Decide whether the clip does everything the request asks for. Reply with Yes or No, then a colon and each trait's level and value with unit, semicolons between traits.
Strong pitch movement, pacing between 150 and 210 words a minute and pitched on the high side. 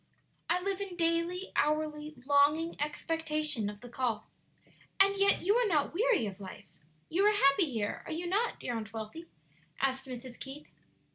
Yes: wide, 5.8 semitones; average, 165 wpm; very high, 305 Hz